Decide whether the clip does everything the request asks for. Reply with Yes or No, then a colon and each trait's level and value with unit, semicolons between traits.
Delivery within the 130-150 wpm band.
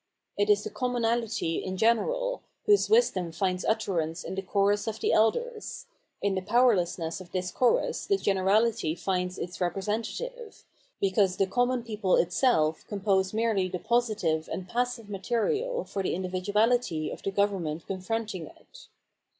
Yes: average, 145 wpm